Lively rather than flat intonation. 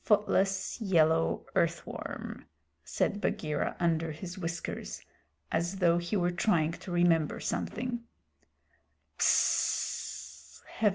No: average, 2.9 semitones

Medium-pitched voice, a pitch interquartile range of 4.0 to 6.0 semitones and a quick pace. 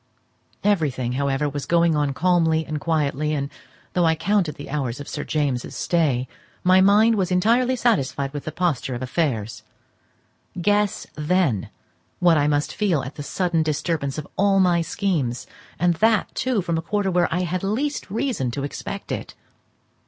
No: medium, 165 Hz; average, 4.9 semitones; average, 165 wpm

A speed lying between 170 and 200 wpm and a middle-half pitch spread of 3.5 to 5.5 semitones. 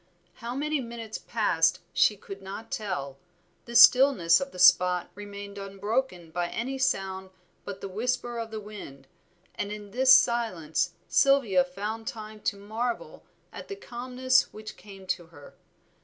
No: average, 150 wpm; average, 4.3 semitones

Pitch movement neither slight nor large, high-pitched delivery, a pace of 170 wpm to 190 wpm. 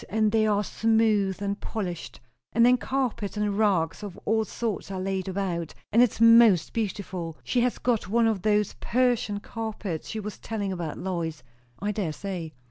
Yes: average, 3.0 semitones; high, 205 Hz; average, 175 wpm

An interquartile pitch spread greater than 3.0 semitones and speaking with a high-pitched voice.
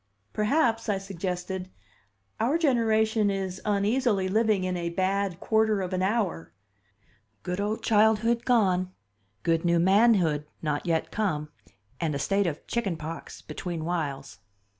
Yes: average, 4.1 semitones; high, 195 Hz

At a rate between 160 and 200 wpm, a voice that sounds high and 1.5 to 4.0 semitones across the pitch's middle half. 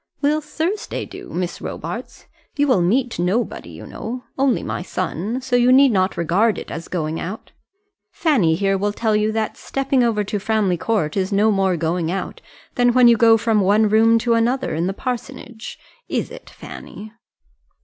No: average, 180 wpm; high, 220 Hz; average, 4.5 semitones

